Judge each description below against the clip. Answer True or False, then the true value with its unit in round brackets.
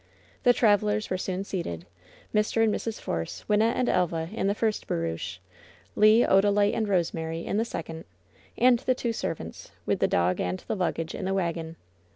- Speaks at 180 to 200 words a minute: True (185 wpm)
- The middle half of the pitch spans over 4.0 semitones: True (4.7 semitones)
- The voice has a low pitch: False (195 Hz)